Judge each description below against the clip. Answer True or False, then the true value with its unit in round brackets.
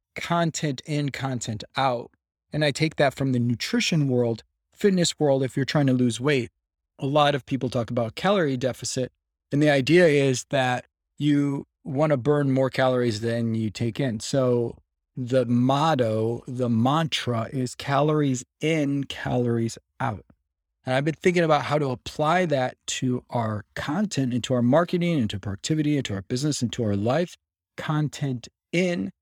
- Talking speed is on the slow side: False (160 wpm)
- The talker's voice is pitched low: True (130 Hz)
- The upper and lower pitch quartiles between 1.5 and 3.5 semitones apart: False (3.9 semitones)